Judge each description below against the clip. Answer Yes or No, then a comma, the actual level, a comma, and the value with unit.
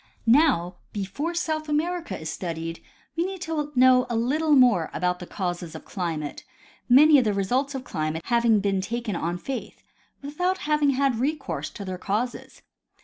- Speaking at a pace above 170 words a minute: No, average, 165 wpm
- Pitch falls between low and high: No, high, 245 Hz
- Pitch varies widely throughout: Yes, wide, 8.3 semitones